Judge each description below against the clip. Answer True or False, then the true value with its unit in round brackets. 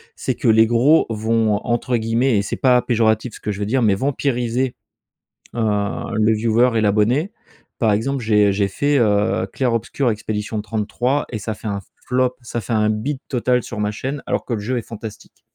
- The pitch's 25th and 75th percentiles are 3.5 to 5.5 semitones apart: False (2.8 semitones)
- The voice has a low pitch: True (115 Hz)